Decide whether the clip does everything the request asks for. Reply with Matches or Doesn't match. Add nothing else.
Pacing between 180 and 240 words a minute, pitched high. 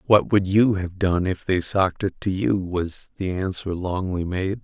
Doesn't match